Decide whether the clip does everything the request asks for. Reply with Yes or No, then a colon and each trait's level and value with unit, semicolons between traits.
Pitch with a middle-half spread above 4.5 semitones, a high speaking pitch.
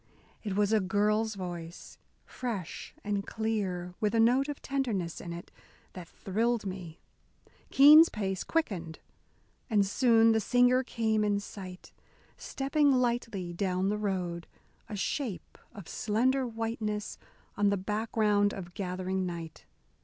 No: average, 3.6 semitones; high, 210 Hz